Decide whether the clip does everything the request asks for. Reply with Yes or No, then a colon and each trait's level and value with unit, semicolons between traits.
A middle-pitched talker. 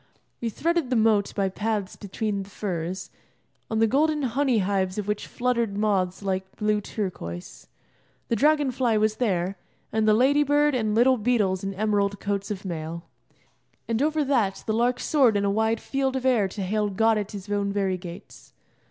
No: high, 215 Hz